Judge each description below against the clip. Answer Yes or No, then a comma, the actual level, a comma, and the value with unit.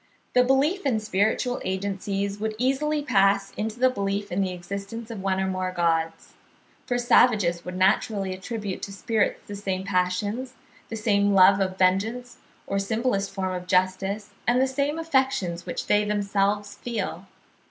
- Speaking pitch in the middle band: No, high, 200 Hz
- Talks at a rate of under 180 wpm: Yes, average, 160 wpm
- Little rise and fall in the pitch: No, average, 3.6 semitones